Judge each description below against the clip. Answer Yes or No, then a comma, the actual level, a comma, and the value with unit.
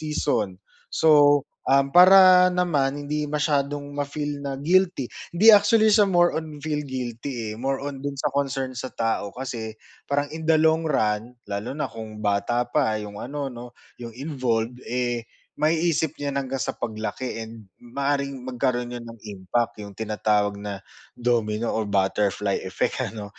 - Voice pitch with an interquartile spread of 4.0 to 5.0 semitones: Yes, average, 4.7 semitones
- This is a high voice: No, low, 130 Hz